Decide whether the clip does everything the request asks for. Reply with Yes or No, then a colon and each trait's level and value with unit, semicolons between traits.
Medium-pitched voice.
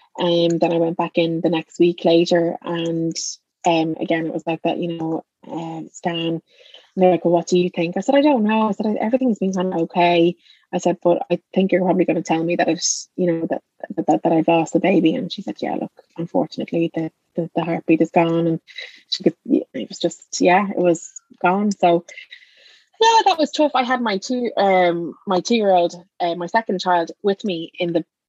Yes: medium, 175 Hz